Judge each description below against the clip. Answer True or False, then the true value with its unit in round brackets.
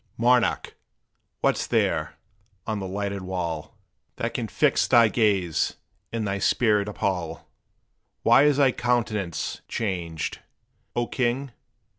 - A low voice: True (105 Hz)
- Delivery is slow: True (115 wpm)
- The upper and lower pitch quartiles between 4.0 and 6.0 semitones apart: True (4.7 semitones)